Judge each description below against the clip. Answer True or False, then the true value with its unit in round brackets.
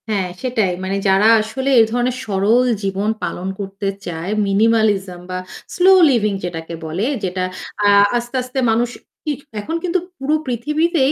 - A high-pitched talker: True (215 Hz)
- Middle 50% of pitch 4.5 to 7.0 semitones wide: True (4.8 semitones)